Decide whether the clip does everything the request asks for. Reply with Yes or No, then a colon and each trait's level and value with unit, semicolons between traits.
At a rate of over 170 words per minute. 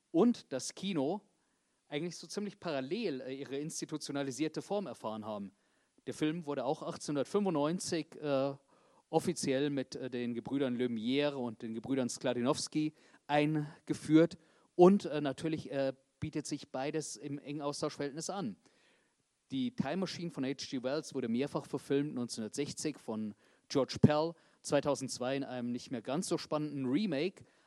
No: average, 130 wpm